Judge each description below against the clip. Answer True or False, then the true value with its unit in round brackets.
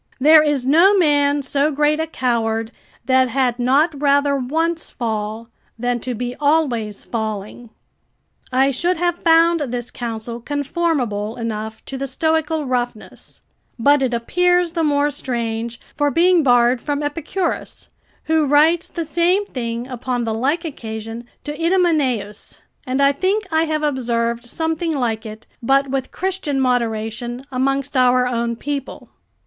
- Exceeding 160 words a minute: False (145 wpm)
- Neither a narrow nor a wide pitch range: True (4.7 semitones)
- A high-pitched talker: True (270 Hz)